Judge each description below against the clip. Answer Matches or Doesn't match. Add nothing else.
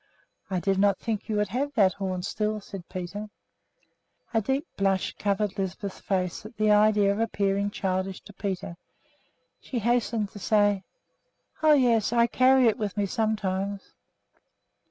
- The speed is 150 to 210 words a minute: Matches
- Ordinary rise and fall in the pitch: Doesn't match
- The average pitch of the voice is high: Matches